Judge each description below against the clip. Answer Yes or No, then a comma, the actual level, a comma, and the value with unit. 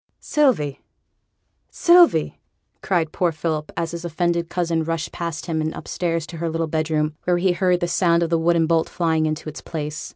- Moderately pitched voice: Yes, medium, 165 Hz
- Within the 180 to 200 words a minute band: Yes, average, 185 wpm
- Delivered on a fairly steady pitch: Yes, narrow, 1.6 semitones